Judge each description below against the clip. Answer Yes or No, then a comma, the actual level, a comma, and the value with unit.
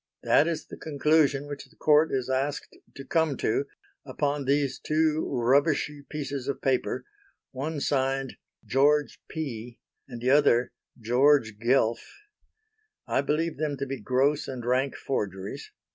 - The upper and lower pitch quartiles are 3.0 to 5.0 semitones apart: No, narrow, 2.5 semitones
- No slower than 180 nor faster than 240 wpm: No, average, 140 wpm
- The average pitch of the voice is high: No, medium, 140 Hz